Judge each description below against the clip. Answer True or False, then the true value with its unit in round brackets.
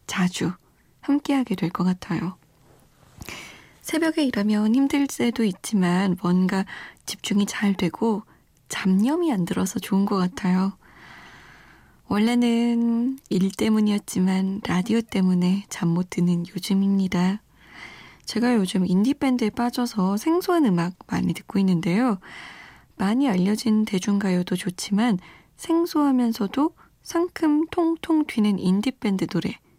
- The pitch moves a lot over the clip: False (4.8 semitones)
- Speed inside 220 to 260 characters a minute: True (255 characters per minute)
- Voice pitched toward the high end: True (205 Hz)